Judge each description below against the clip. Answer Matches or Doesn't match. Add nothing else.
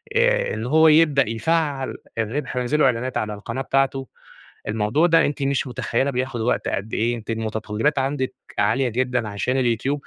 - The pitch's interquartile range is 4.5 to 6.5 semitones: Doesn't match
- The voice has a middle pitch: Doesn't match